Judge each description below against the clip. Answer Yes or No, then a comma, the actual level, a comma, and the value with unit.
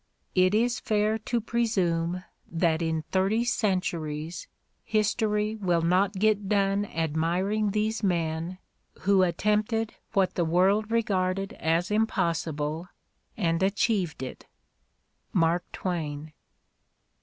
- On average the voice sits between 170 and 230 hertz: Yes, high, 190 Hz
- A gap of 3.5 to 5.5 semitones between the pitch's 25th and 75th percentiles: Yes, average, 4.1 semitones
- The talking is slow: Yes, slow, 105 wpm